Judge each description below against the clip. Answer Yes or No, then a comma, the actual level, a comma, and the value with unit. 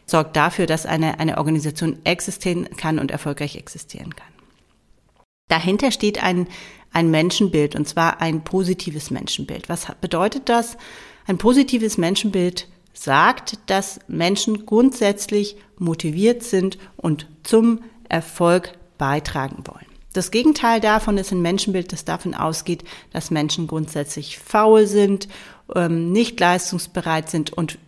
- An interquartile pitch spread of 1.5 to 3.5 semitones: No, average, 4.2 semitones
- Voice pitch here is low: No, medium, 180 Hz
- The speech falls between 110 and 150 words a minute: Yes, slow, 125 wpm